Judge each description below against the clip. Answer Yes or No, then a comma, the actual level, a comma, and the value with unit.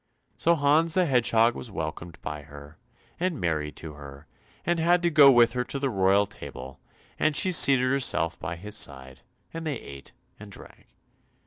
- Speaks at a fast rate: No, average, 180 wpm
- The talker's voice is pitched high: No, low, 110 Hz